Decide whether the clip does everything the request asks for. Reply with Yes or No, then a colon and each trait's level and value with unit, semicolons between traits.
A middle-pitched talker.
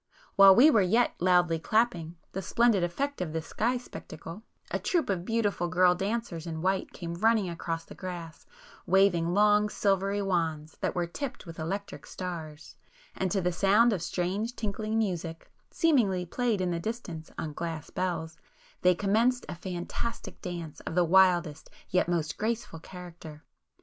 Yes: medium, 180 Hz